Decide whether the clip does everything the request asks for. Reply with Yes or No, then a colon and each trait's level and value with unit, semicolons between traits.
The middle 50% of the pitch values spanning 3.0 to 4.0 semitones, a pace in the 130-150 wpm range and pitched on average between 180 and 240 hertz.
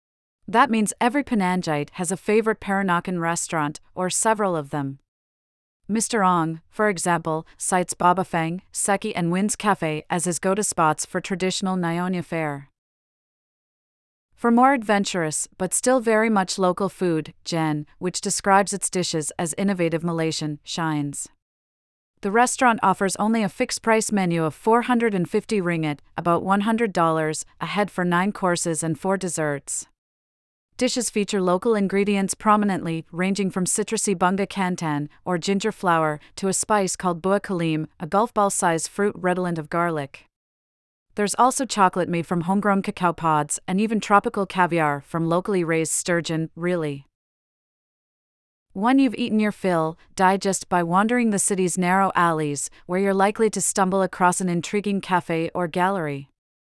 Yes: average, 3.5 semitones; average, 145 wpm; medium, 185 Hz